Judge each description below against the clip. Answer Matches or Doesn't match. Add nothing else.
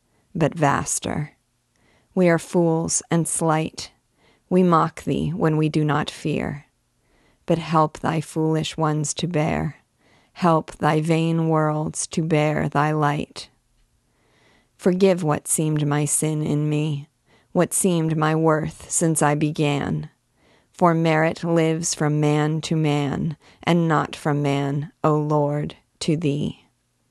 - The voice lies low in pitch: Doesn't match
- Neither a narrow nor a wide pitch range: Doesn't match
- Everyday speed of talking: Doesn't match